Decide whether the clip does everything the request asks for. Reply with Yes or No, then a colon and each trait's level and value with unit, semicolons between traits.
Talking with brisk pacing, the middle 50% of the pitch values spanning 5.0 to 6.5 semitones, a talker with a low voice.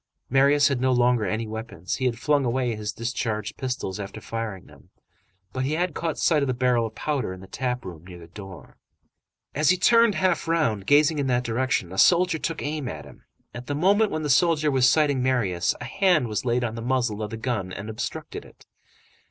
Yes: fast, 220 wpm; average, 5.3 semitones; low, 125 Hz